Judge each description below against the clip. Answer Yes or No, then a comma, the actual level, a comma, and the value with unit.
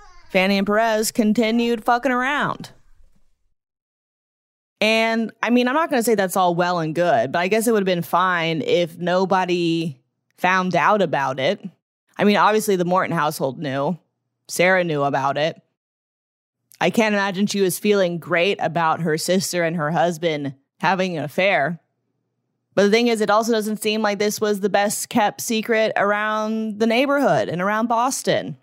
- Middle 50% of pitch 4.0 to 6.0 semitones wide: Yes, average, 4.4 semitones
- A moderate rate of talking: Yes, average, 170 wpm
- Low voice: No, high, 190 Hz